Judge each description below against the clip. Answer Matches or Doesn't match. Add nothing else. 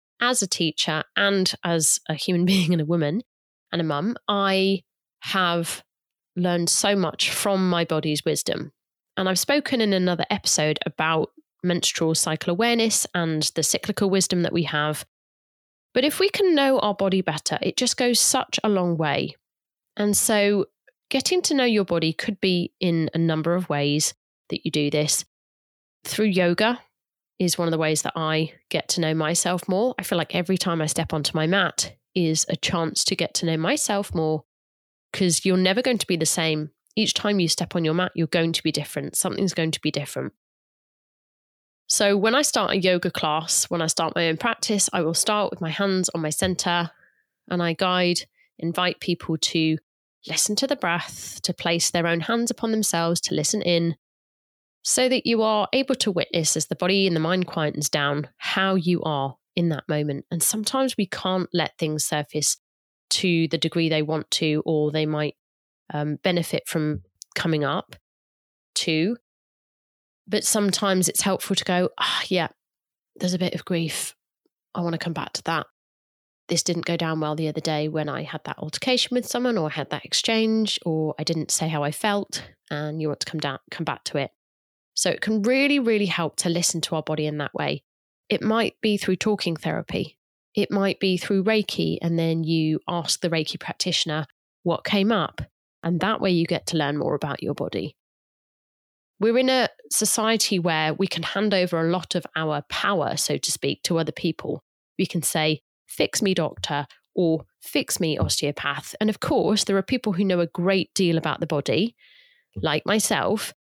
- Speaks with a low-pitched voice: Doesn't match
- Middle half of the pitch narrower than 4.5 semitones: Matches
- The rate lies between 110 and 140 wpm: Doesn't match